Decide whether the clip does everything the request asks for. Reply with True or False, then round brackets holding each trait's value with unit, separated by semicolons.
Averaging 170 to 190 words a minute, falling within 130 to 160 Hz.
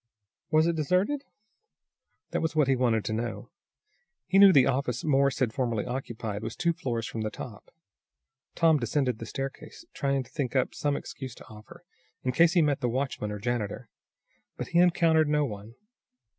True (180 wpm; 135 Hz)